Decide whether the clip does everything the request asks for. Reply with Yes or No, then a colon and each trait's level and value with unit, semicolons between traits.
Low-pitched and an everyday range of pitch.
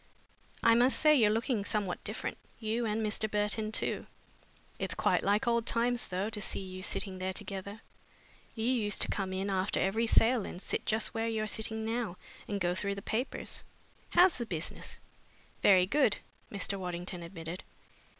No: high, 210 Hz; average, 3.0 semitones